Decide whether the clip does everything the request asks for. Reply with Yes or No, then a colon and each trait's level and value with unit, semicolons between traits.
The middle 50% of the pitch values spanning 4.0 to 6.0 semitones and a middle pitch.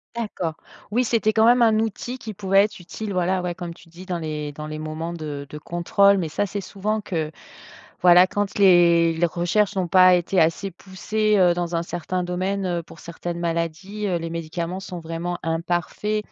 No: average, 2.9 semitones; medium, 180 Hz